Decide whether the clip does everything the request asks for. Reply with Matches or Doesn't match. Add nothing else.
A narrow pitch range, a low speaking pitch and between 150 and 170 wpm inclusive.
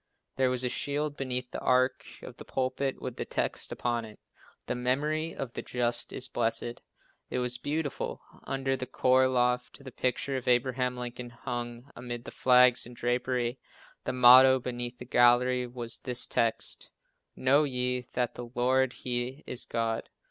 Matches